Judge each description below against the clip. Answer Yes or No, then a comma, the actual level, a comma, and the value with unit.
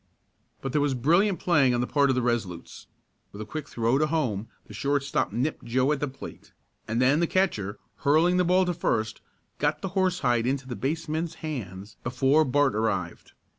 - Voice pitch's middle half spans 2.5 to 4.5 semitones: No, average, 5.0 semitones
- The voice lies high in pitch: No, low, 135 Hz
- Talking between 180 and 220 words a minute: Yes, average, 190 wpm